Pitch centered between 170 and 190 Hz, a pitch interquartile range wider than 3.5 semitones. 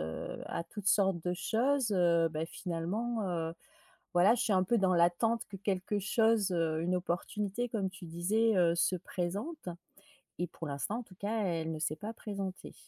Yes: medium, 185 Hz; average, 4.0 semitones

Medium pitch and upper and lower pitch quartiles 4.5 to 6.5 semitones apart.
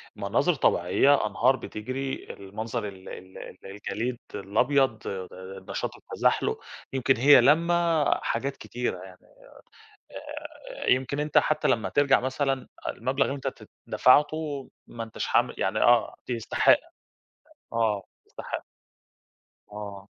No: low, 120 Hz; average, 4.9 semitones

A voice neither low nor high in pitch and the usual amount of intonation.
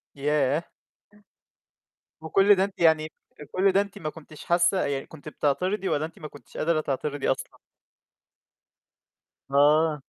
Yes: medium, 155 Hz; average, 3.4 semitones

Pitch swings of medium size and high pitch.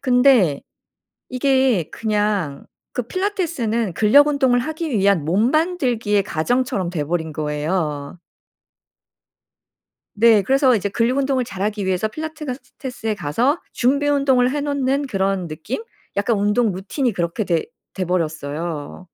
No: wide, 6.6 semitones; high, 220 Hz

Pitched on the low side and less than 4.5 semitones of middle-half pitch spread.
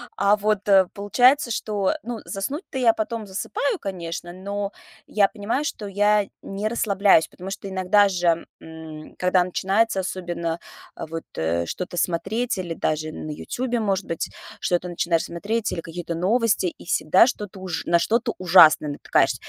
No: high, 190 Hz; average, 3.7 semitones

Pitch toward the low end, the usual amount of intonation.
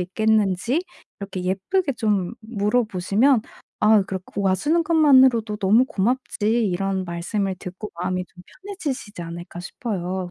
No: high, 205 Hz; average, 4.4 semitones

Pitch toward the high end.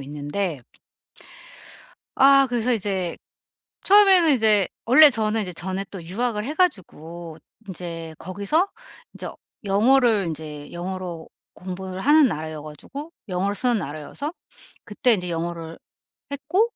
Yes: high, 195 Hz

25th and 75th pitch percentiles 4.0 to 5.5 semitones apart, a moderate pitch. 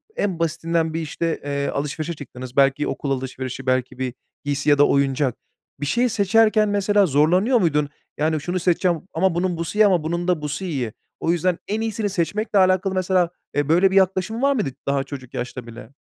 Yes: average, 5.2 semitones; medium, 165 Hz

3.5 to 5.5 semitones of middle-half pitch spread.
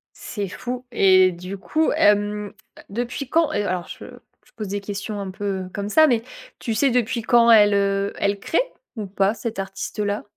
No: average, 2.9 semitones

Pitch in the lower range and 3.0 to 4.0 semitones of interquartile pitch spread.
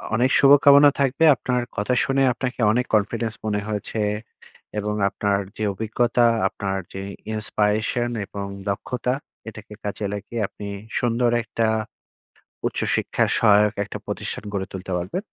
Yes: low, 110 Hz; average, 3.3 semitones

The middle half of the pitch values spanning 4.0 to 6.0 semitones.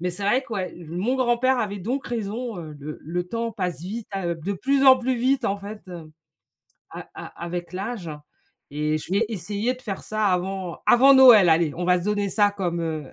Yes: average, 5.1 semitones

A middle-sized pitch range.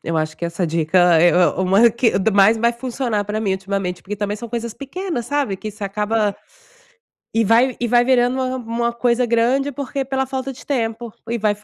Yes: average, 3.7 semitones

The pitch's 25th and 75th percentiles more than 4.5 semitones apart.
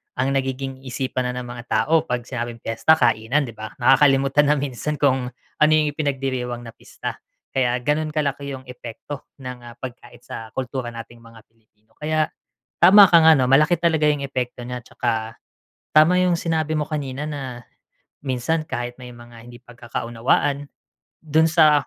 No: average, 3.7 semitones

